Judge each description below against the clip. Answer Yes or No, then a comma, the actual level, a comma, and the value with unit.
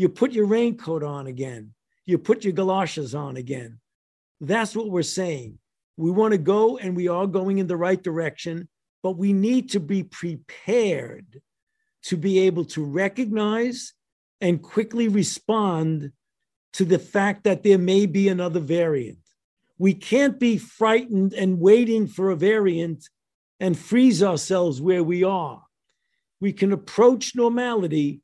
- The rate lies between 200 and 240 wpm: No, average, 150 wpm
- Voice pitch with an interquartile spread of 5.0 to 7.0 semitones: No, average, 4.3 semitones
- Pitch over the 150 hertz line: Yes, high, 190 Hz